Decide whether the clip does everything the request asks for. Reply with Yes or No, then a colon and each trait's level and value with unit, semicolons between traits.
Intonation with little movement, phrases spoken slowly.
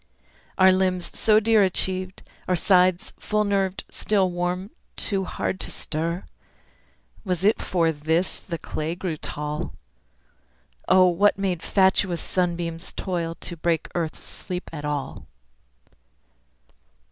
Yes: narrow, 2.2 semitones; slow, 125 wpm